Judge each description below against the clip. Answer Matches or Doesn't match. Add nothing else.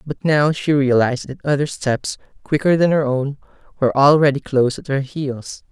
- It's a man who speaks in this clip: Matches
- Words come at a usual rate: Matches